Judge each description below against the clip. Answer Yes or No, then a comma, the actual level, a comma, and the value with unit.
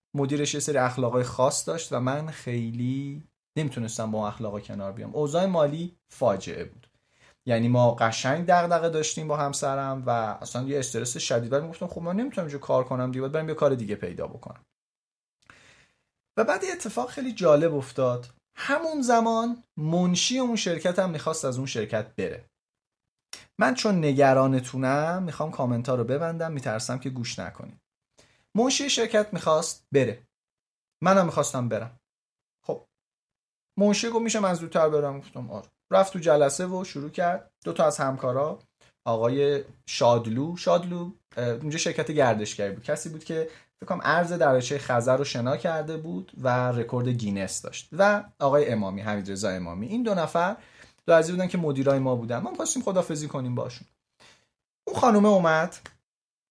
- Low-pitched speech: No, medium, 145 Hz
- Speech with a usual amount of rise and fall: No, wide, 5.8 semitones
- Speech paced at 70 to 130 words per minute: No, fast, 155 wpm